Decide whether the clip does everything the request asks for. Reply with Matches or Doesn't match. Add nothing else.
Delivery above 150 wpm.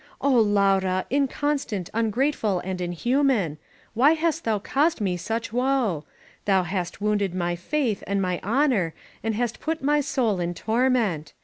Doesn't match